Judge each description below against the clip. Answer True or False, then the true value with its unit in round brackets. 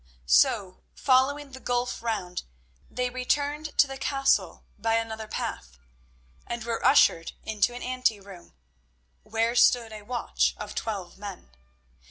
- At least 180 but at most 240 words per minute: False (135 wpm)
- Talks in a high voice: True (230 Hz)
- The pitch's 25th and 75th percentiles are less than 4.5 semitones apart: True (3.8 semitones)